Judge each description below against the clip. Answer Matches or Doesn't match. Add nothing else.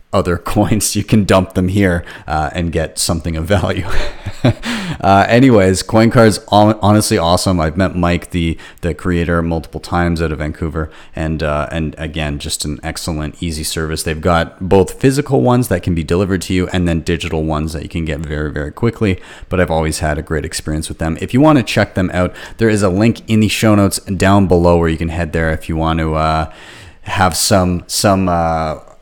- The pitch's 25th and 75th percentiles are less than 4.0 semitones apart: Matches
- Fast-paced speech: Matches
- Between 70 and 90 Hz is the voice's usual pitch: Matches